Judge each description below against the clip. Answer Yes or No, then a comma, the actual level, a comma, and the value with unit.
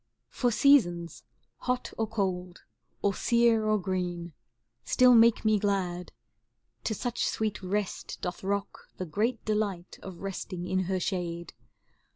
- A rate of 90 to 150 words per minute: Yes, average, 140 wpm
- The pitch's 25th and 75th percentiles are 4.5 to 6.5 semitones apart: No, average, 3.5 semitones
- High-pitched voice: Yes, high, 195 Hz